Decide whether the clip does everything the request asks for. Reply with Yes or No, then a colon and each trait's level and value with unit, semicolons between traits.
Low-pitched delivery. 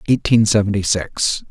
Yes: low, 105 Hz